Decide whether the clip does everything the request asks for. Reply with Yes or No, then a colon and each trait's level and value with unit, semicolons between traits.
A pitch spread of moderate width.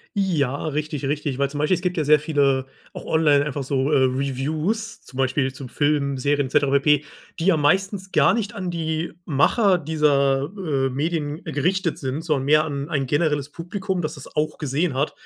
Yes: average, 3.0 semitones